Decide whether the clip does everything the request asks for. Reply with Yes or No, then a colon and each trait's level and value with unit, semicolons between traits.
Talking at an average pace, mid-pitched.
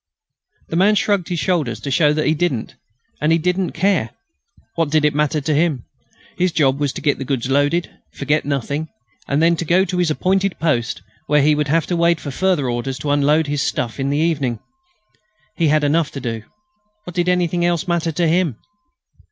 No: fast, 210 wpm; medium, 155 Hz